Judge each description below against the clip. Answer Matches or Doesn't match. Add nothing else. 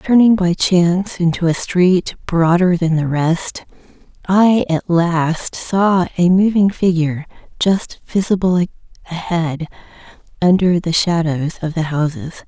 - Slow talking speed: Matches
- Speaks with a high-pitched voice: Doesn't match